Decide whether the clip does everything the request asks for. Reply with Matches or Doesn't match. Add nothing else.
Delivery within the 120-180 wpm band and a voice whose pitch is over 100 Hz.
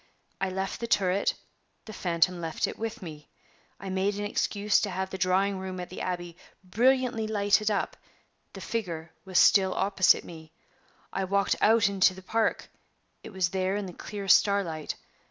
Matches